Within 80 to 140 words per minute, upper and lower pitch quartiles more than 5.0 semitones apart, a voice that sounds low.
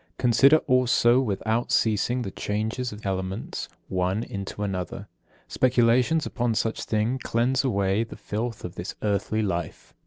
No: slow, 135 wpm; average, 3.7 semitones; low, 110 Hz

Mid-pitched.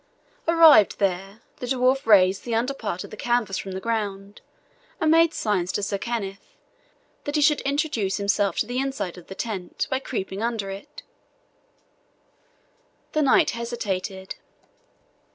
No: high, 220 Hz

